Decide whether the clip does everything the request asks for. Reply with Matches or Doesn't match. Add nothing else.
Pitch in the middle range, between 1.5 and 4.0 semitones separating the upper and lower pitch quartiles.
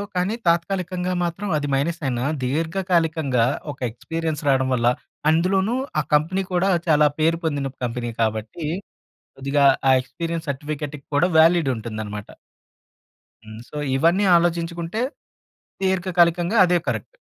Doesn't match